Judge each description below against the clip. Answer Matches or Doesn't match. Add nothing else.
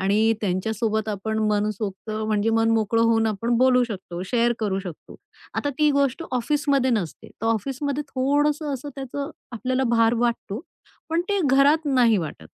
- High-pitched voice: Matches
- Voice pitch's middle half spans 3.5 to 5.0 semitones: Matches